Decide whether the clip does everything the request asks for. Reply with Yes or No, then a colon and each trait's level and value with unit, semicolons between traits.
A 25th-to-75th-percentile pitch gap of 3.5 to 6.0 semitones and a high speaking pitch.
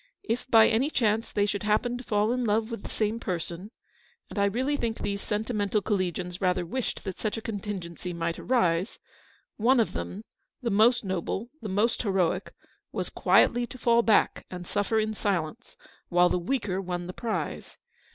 Yes: average, 3.8 semitones; high, 210 Hz